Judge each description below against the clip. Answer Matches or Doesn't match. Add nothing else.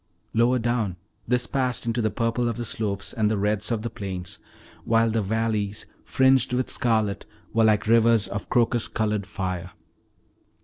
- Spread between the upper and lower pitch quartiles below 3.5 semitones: Matches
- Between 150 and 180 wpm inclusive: Matches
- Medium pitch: Doesn't match